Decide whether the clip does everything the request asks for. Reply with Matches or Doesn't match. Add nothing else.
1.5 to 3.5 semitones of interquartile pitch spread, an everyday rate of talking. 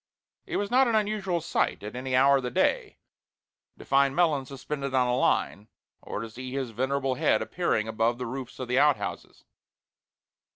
Matches